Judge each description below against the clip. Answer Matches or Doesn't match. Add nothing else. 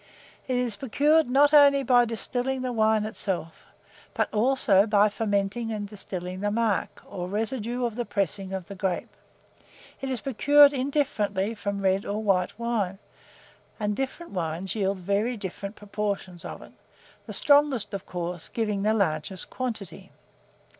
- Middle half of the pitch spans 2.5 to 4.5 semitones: Matches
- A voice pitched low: Doesn't match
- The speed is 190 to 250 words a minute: Doesn't match